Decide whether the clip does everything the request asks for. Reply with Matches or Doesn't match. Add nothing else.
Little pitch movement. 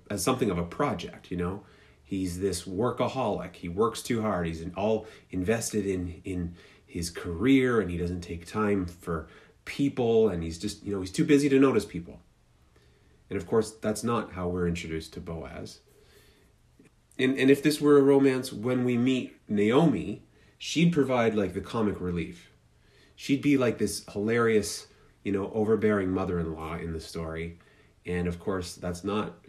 Doesn't match